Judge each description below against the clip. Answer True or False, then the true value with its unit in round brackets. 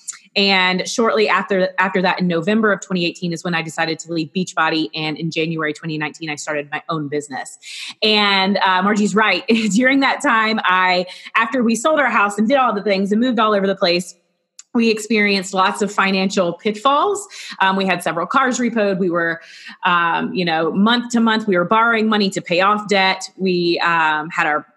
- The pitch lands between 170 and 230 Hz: True (190 Hz)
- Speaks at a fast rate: False (195 wpm)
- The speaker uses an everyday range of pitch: True (4.1 semitones)